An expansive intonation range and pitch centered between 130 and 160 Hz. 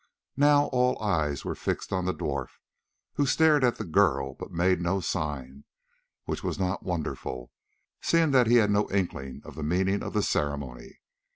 No: wide, 7.7 semitones; very low, 95 Hz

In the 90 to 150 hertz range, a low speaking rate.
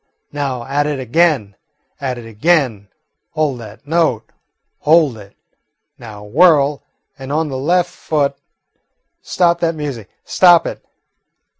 Yes: medium, 140 Hz; slow, 125 wpm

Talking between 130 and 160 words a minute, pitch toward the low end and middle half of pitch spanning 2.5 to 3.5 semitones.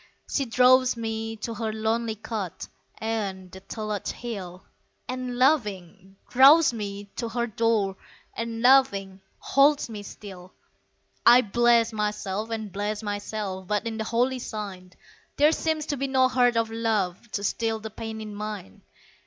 No: average, 150 wpm; high, 220 Hz; average, 2.9 semitones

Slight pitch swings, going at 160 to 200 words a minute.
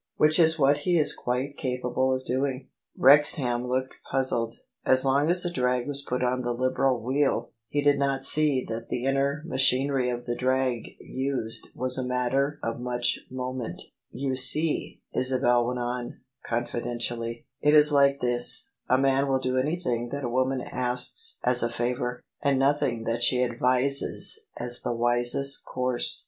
Yes: narrow, 2.2 semitones; average, 170 wpm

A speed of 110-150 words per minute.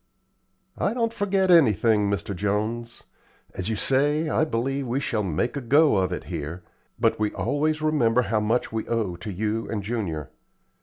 No: average, 170 wpm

